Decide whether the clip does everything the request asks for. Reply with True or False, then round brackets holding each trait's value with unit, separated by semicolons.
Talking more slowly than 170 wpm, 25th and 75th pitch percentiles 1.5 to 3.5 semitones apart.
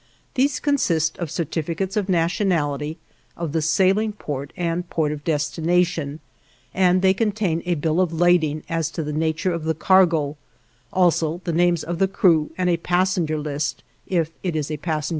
False (175 wpm; 2.8 semitones)